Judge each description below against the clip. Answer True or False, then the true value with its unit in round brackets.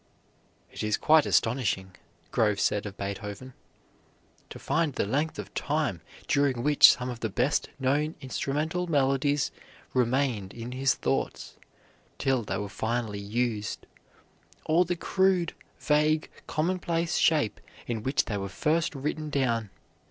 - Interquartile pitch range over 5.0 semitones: True (5.6 semitones)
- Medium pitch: False (130 Hz)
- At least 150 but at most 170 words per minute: False (135 wpm)